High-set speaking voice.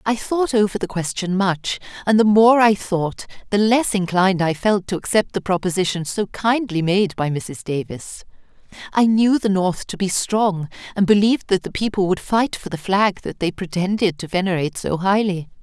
Yes: high, 195 Hz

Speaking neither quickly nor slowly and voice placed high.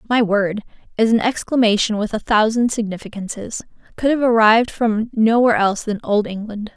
Yes: average, 160 wpm; high, 220 Hz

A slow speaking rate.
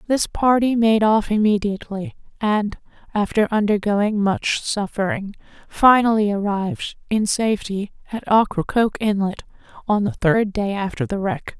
Yes: slow, 125 wpm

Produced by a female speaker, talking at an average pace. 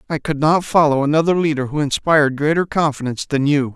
No: male; average, 190 wpm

